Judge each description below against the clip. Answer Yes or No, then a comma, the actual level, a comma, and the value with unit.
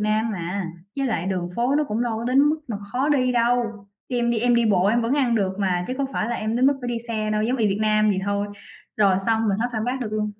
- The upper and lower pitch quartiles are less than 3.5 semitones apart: Yes, average, 2.9 semitones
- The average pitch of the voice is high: Yes, high, 225 Hz